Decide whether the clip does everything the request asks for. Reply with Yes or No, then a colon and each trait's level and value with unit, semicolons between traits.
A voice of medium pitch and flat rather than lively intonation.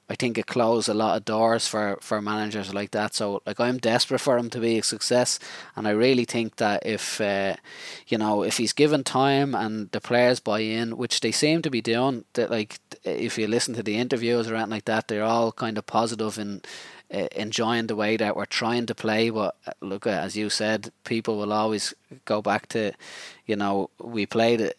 No: low, 115 Hz; narrow, 1.8 semitones